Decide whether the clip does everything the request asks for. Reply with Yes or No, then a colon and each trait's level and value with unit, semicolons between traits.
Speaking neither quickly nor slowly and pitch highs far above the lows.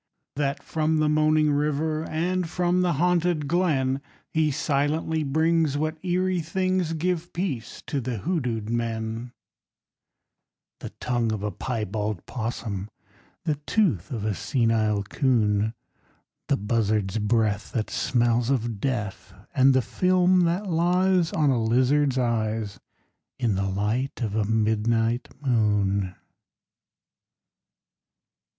No: slow, 120 wpm; wide, 6.3 semitones